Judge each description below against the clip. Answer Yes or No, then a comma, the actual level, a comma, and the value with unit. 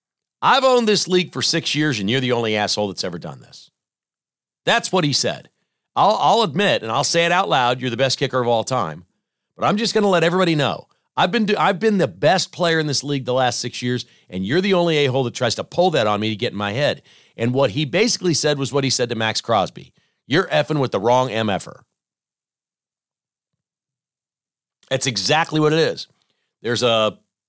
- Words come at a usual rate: No, fast, 225 wpm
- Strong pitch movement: Yes, wide, 5.9 semitones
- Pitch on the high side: No, low, 135 Hz